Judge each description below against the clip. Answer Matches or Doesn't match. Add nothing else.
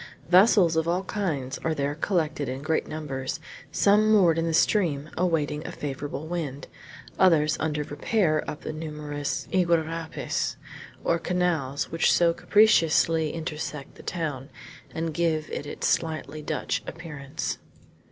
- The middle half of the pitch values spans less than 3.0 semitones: Matches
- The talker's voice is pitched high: Doesn't match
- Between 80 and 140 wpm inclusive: Matches